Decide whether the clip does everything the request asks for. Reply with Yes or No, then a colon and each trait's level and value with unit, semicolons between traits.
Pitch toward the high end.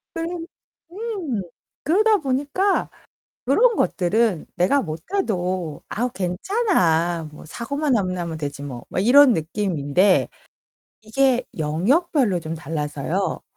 Yes: high, 200 Hz